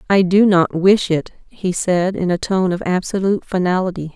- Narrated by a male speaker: No, female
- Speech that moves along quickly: No, average, 190 wpm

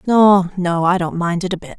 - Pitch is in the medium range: Yes, medium, 180 Hz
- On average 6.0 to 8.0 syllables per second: No, 5.0 syllables/s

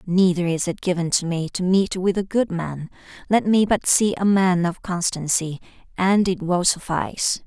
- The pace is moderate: Yes, average, 195 wpm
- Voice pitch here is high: No, medium, 180 Hz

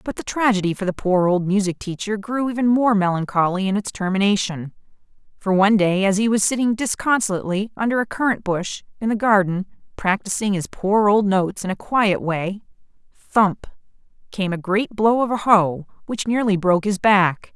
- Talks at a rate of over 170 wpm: Yes, average, 180 wpm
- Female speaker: Yes, female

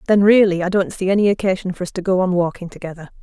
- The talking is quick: Yes, fast, 260 wpm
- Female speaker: Yes, female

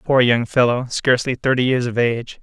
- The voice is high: No, low, 125 Hz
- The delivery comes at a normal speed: Yes, average, 175 wpm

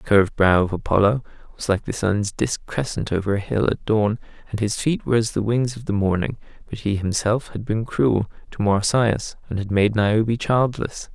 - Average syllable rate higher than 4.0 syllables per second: Yes, 5.1 syllables/s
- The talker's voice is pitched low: Yes, low, 105 Hz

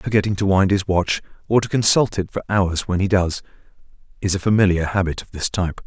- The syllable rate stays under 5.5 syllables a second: No, 5.9 syllables/s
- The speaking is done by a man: Yes, male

